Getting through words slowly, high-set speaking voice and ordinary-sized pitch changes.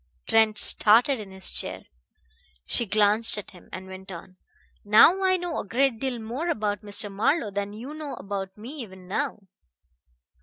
No: average, 165 wpm; high, 215 Hz; average, 4.8 semitones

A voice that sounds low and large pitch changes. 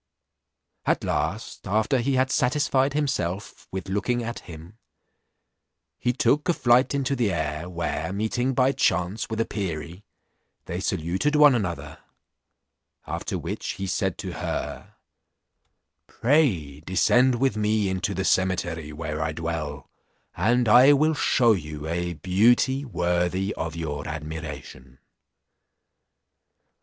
Yes: very low, 95 Hz; wide, 7.0 semitones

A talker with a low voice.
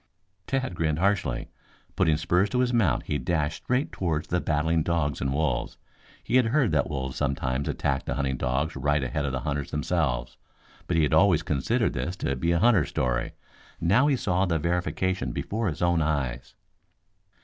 Yes: very low, 80 Hz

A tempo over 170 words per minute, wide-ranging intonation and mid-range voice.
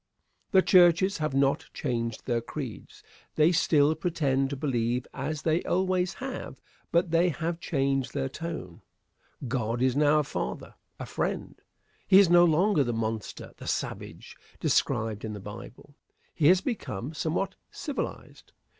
No: average, 145 wpm; wide, 5.8 semitones; medium, 150 Hz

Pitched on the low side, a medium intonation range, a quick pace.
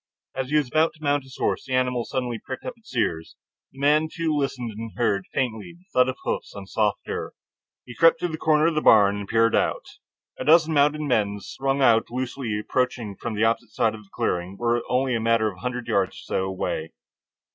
Yes: low, 125 Hz; average, 4.7 semitones; fast, 225 wpm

